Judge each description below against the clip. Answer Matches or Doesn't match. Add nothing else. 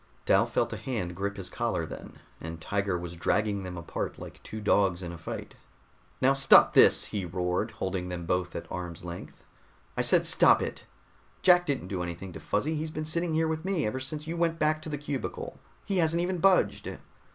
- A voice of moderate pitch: Doesn't match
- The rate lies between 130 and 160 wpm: Doesn't match